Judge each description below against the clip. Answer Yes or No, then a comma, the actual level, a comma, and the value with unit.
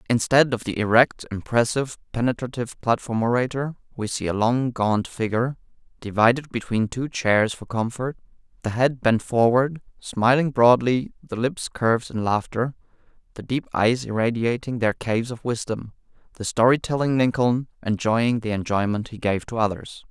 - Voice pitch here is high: No, low, 120 Hz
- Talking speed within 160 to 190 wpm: No, average, 150 wpm